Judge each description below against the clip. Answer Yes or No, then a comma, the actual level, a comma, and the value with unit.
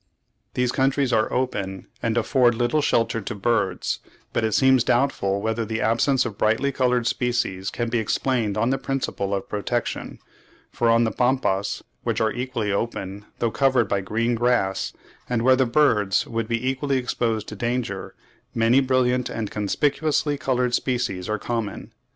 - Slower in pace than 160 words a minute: No, average, 165 wpm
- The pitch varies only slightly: No, average, 3.1 semitones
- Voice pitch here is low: Yes, low, 120 Hz